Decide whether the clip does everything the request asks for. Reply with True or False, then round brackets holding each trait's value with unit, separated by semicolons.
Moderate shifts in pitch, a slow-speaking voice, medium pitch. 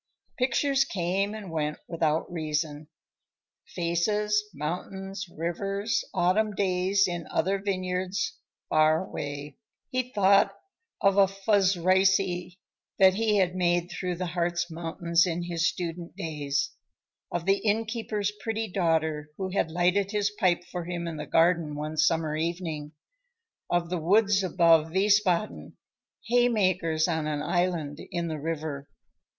True (3.3 semitones; 125 wpm; 180 Hz)